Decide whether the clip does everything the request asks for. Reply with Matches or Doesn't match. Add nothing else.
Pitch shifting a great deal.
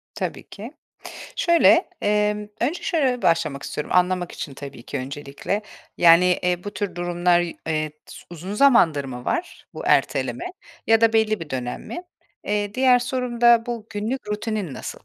Matches